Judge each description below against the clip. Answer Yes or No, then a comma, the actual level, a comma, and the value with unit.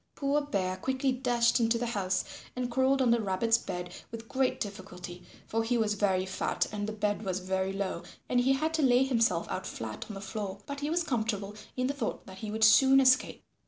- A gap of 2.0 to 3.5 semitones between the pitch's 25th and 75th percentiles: No, average, 5.0 semitones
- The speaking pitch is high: Yes, high, 225 Hz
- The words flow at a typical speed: No, fast, 215 wpm